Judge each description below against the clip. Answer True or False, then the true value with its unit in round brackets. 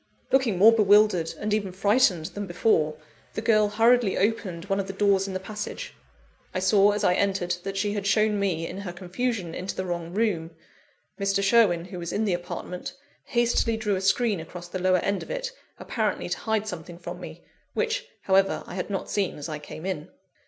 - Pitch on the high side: True (195 Hz)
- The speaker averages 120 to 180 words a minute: False (200 wpm)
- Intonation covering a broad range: False (3.1 semitones)